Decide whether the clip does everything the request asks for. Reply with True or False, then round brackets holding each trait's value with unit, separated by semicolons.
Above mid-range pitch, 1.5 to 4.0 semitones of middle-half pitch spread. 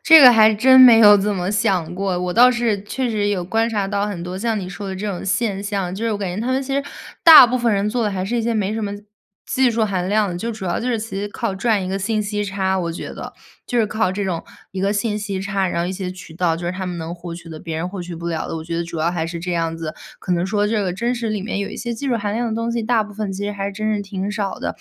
True (200 Hz; 3.5 semitones)